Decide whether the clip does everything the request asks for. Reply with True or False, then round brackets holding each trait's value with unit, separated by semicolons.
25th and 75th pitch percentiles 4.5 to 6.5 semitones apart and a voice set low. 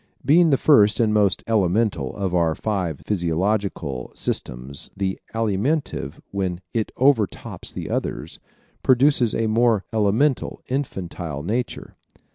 True (4.9 semitones; 105 Hz)